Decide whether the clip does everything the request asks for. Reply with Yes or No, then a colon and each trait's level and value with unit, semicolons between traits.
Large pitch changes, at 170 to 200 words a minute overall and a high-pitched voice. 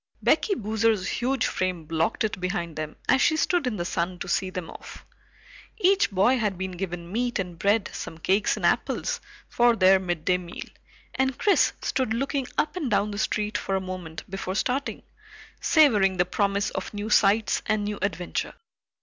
No: average, 4.3 semitones; average, 180 wpm; high, 200 Hz